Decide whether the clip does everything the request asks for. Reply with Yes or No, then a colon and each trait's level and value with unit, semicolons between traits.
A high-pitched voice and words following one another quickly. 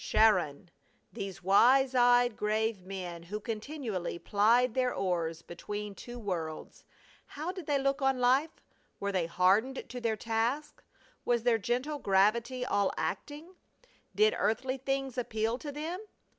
No: high, 230 Hz; average, 140 wpm